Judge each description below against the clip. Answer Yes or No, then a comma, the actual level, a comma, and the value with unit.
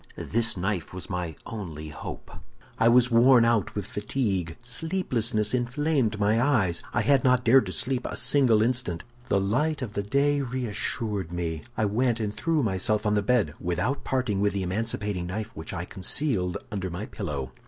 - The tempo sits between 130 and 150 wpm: No, average, 175 wpm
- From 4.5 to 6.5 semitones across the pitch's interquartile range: Yes, average, 5.1 semitones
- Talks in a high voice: No, low, 110 Hz